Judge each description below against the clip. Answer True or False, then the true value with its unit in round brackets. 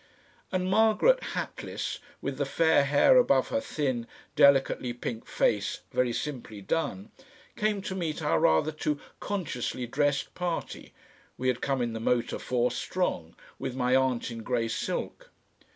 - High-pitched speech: False (135 Hz)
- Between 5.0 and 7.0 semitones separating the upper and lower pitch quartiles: True (5.4 semitones)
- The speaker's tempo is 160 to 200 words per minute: False (150 wpm)